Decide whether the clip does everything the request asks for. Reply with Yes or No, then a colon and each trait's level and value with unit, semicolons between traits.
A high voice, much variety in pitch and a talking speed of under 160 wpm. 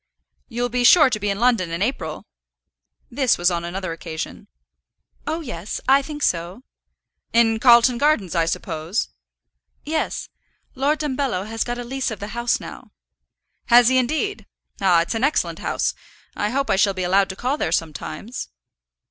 No: high, 230 Hz; wide, 6.1 semitones; average, 165 wpm